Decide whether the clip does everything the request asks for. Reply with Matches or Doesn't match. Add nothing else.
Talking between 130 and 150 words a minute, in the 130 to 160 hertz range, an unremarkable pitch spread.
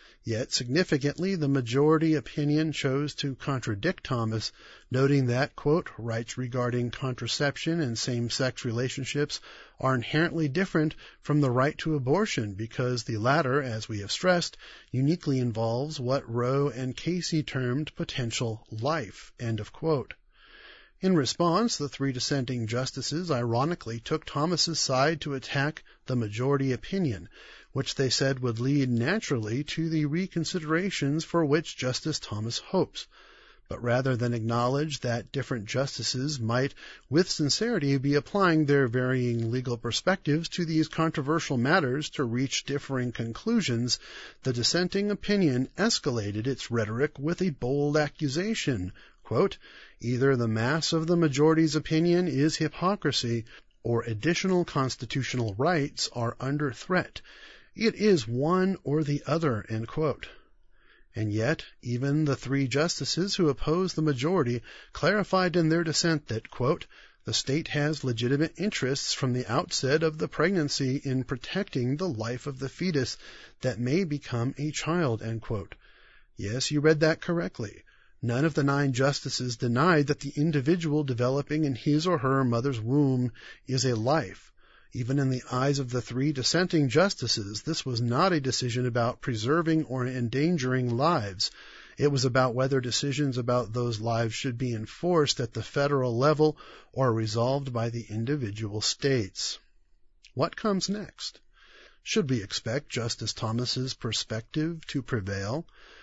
Matches